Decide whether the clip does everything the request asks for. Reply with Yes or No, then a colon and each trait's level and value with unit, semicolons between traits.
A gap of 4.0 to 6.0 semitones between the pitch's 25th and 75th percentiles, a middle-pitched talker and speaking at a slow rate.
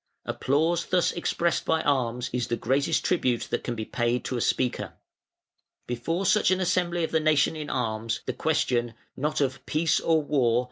No: average, 5.1 semitones; medium, 145 Hz; average, 180 wpm